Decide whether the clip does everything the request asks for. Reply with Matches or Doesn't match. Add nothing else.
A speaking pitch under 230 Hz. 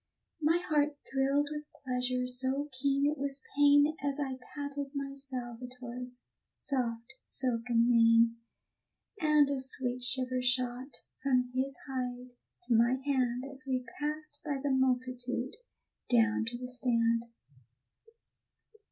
Doesn't match